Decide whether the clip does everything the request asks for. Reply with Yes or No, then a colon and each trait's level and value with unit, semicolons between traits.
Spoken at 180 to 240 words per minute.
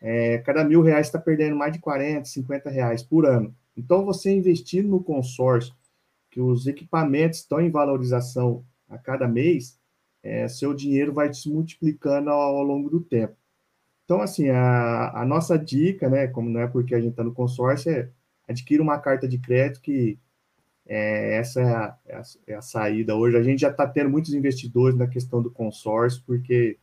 Yes: fast, 185 wpm